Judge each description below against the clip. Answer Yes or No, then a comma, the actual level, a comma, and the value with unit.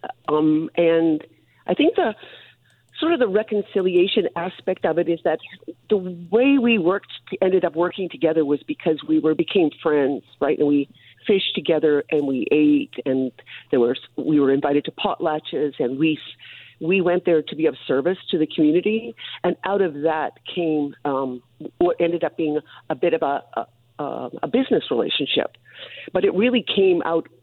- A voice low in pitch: No, medium, 165 Hz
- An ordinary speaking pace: Yes, average, 175 wpm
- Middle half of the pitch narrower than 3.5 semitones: No, average, 3.8 semitones